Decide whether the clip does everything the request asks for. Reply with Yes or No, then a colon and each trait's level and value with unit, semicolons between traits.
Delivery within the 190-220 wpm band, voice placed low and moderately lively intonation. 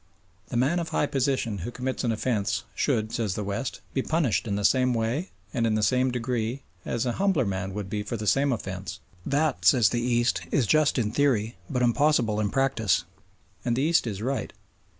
Yes: fast, 205 wpm; low, 120 Hz; average, 4.0 semitones